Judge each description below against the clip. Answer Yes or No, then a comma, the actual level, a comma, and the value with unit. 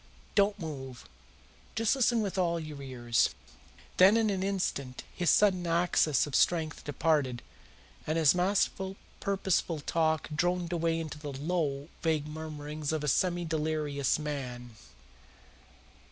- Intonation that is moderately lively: Yes, average, 3.6 semitones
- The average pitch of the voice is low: No, medium, 160 Hz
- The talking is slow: Yes, slow, 130 wpm